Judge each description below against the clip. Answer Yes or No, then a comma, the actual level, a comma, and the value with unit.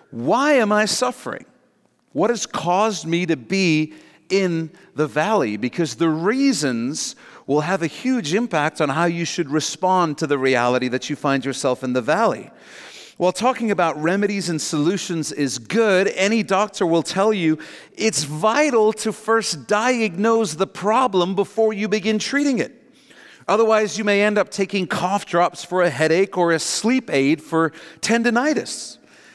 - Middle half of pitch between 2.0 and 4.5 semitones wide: No, average, 5.3 semitones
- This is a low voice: No, medium, 185 Hz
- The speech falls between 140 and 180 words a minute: Yes, average, 160 wpm